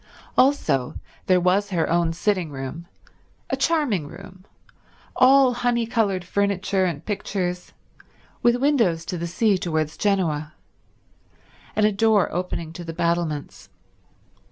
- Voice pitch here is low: No, medium, 185 Hz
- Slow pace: Yes, slow, 130 wpm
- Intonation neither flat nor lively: Yes, average, 4.1 semitones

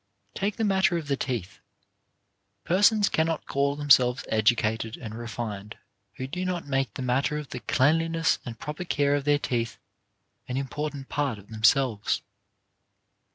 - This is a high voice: No, low, 135 Hz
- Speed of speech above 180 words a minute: No, average, 150 wpm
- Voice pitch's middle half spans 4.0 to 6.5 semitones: Yes, average, 4.6 semitones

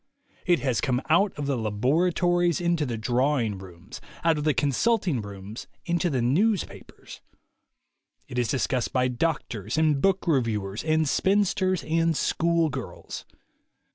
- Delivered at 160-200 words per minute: No, average, 140 wpm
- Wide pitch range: Yes, wide, 6.0 semitones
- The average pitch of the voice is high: No, medium, 145 Hz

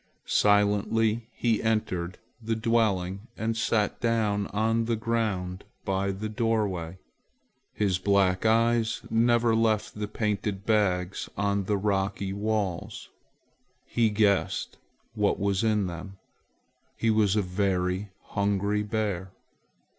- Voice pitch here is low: Yes, low, 105 Hz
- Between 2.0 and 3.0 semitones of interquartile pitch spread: Yes, narrow, 2.5 semitones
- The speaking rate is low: Yes, slow, 115 wpm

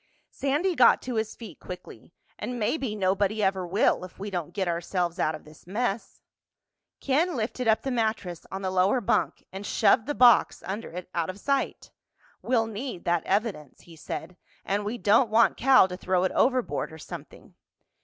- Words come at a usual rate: Yes, average, 185 wpm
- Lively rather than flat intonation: No, average, 4.8 semitones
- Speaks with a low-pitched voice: No, high, 205 Hz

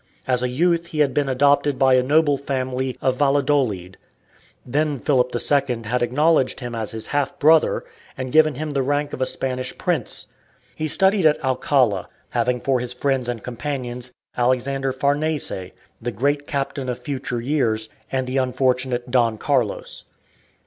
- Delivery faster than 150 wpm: Yes, average, 160 wpm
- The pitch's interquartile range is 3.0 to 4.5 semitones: No, narrow, 2.5 semitones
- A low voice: Yes, low, 130 Hz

